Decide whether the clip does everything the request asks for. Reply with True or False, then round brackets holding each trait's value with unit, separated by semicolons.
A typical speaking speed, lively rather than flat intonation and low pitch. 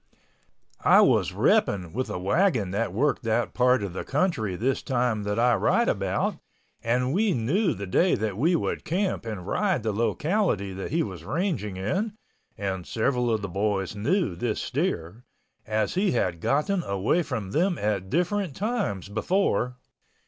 True (165 wpm; 9.0 semitones; 115 Hz)